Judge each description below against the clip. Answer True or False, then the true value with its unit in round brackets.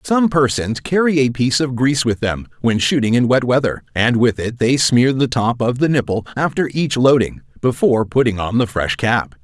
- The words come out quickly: True (210 wpm)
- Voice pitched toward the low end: True (125 Hz)